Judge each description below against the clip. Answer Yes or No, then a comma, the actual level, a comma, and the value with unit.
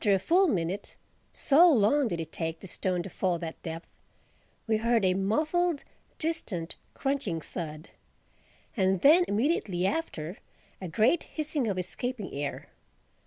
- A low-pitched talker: No, high, 200 Hz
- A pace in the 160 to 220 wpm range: No, average, 140 wpm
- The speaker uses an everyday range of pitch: No, wide, 8.4 semitones